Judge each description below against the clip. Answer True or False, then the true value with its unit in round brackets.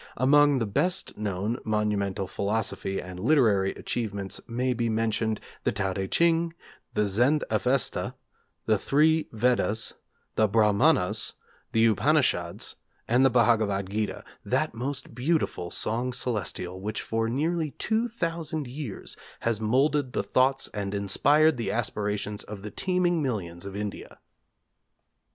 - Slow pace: True (130 wpm)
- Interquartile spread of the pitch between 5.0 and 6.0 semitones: True (5.6 semitones)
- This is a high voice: False (115 Hz)